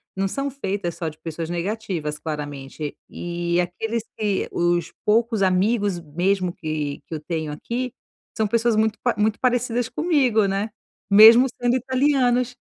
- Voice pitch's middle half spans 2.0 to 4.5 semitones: No, wide, 5.5 semitones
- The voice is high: Yes, high, 200 Hz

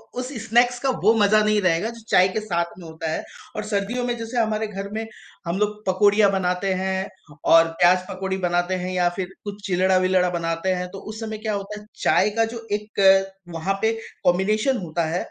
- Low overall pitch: No, high, 195 Hz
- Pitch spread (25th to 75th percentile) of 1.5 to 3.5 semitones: Yes, average, 2.9 semitones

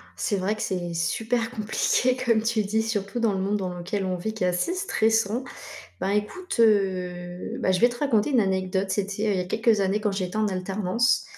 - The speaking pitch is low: No, high, 205 Hz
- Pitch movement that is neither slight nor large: Yes, average, 3.2 semitones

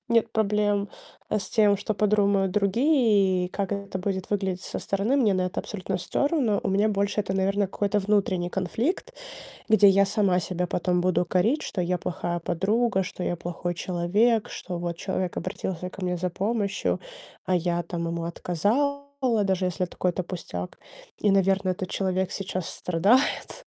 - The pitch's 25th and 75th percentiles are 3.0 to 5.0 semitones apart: No, narrow, 2.5 semitones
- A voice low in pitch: No, high, 195 Hz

